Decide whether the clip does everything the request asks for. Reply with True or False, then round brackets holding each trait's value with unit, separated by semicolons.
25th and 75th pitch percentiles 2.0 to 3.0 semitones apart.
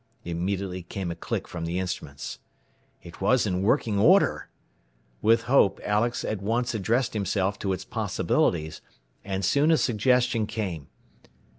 False (4.3 semitones)